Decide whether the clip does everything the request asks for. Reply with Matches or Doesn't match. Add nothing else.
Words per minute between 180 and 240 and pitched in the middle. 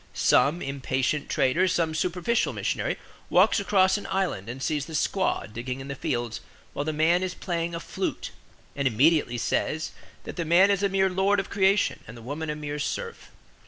Matches